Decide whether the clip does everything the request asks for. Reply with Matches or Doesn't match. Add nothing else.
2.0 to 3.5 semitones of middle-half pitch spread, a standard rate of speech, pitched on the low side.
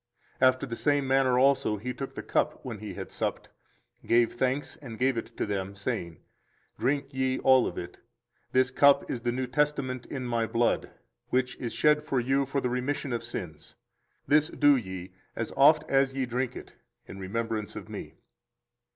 Matches